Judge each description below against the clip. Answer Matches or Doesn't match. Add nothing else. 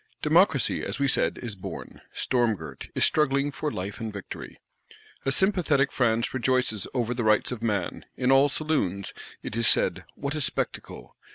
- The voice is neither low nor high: Doesn't match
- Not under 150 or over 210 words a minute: Matches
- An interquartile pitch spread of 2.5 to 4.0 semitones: Doesn't match